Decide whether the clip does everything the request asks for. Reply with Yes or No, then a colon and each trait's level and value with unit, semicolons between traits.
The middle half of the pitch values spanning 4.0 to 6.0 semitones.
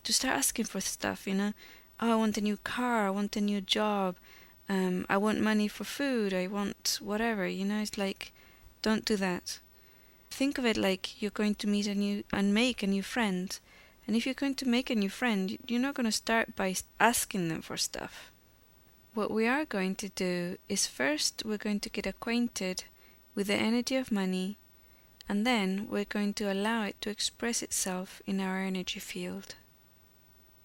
No: narrow, 2.6 semitones